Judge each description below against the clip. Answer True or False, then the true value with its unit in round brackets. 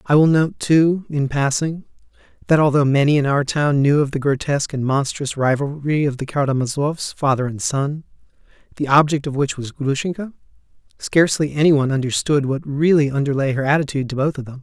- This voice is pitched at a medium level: True (145 Hz)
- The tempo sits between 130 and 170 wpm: False (180 wpm)